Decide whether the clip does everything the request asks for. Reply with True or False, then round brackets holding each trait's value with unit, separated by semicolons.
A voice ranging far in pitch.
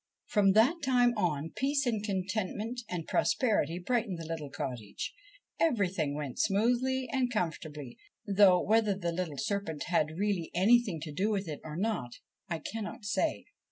True (5.8 semitones)